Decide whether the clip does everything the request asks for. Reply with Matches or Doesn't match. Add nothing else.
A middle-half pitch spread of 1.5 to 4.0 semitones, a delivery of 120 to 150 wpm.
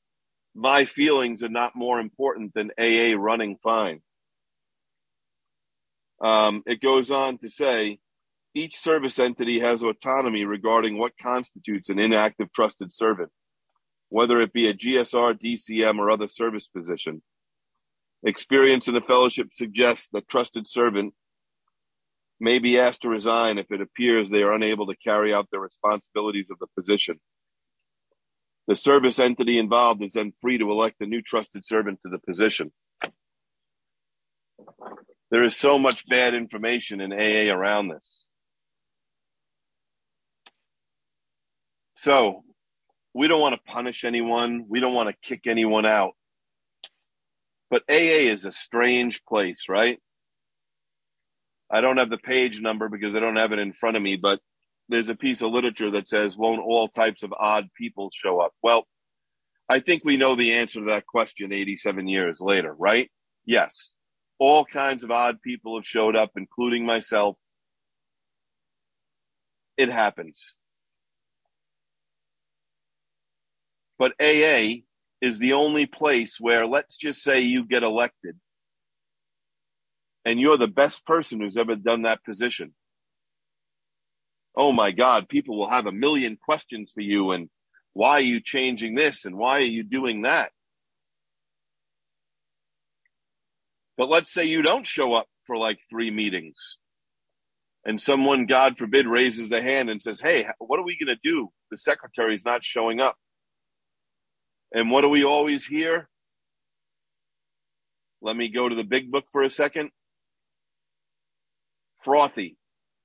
Matches